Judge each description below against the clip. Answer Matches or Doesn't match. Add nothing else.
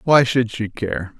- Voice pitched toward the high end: Doesn't match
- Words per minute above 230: Doesn't match